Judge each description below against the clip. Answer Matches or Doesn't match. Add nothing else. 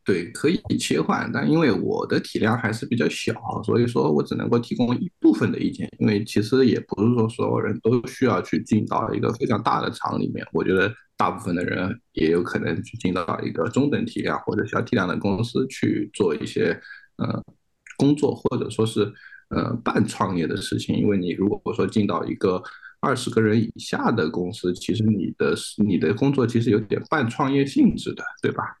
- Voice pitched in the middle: Doesn't match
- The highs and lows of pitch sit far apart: Doesn't match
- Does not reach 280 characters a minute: Doesn't match